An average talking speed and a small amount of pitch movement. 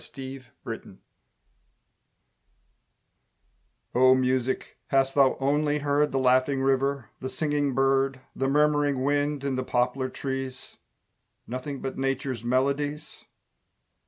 No: slow, 105 wpm; narrow, 1.6 semitones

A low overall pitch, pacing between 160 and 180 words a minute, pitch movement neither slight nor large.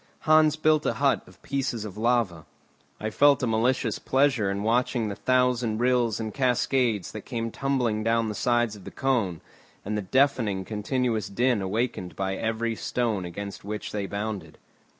Yes: low, 115 Hz; average, 170 wpm; average, 3.4 semitones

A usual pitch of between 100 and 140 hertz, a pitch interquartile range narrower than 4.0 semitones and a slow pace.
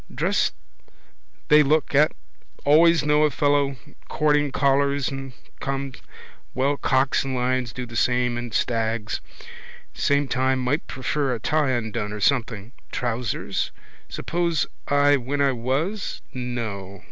Yes: low, 135 Hz; average, 2.9 semitones; slow, 130 wpm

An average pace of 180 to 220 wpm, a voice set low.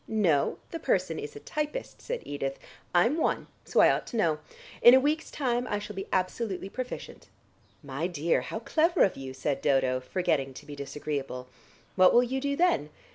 No: average, 185 wpm; medium, 185 Hz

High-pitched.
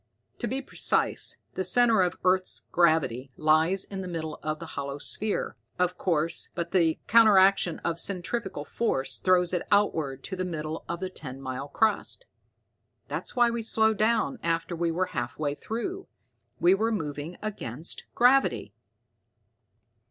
No: medium, 180 Hz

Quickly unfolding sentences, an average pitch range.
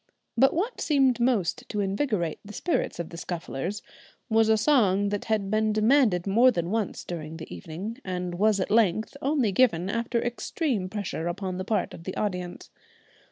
No: average, 175 wpm; average, 4.4 semitones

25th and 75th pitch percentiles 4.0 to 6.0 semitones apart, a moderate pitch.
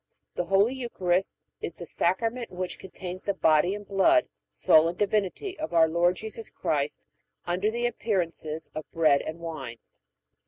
Yes: average, 4.4 semitones; medium, 180 Hz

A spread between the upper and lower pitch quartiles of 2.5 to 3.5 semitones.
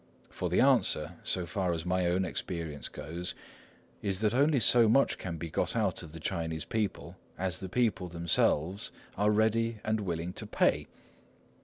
No: average, 4.4 semitones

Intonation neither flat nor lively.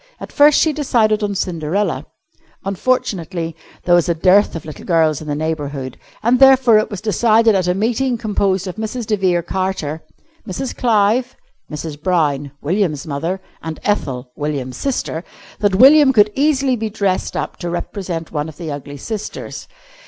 No: wide, 5.7 semitones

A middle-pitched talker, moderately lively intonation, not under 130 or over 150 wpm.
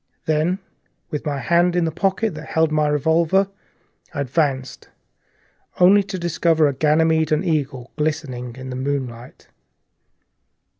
Yes: medium, 155 Hz; average, 3.7 semitones; slow, 135 wpm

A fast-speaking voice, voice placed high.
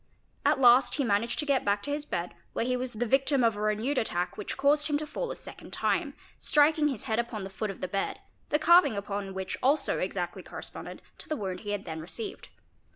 Yes: fast, 230 wpm; high, 235 Hz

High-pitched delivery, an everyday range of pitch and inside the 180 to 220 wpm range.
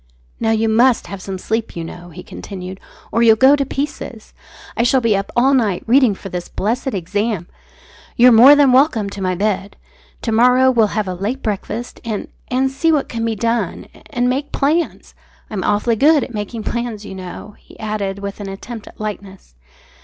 Yes: high, 225 Hz; average, 3.9 semitones; average, 195 wpm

